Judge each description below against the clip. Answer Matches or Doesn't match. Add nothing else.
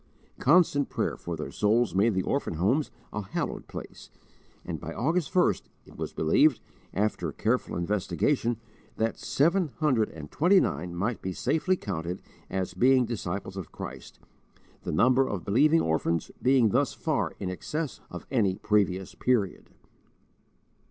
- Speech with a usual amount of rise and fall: Doesn't match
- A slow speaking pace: Doesn't match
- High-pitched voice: Doesn't match